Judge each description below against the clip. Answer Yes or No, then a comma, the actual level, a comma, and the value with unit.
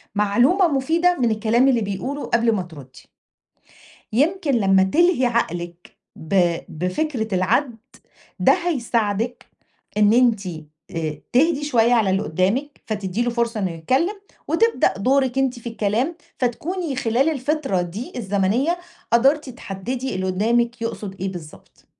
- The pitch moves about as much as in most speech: No, wide, 5.8 semitones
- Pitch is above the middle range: Yes, high, 235 Hz